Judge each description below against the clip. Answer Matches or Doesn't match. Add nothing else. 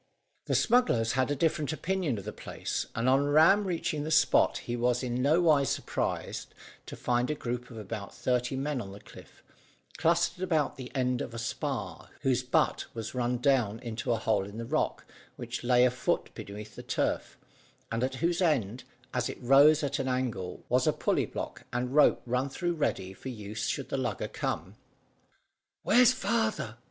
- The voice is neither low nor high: Doesn't match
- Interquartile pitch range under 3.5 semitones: Doesn't match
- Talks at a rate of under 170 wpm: Doesn't match